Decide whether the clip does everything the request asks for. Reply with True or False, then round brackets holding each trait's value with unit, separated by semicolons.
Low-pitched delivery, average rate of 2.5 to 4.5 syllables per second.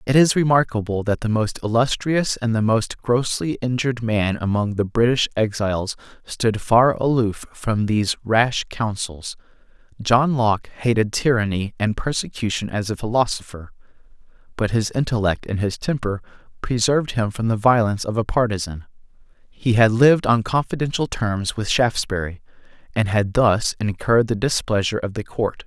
False (115 Hz; 5.1 syllables/s)